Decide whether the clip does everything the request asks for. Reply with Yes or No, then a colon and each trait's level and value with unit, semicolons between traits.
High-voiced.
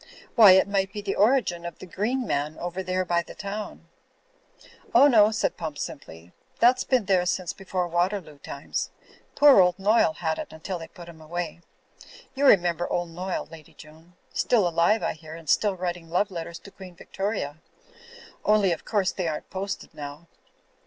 No: medium, 180 Hz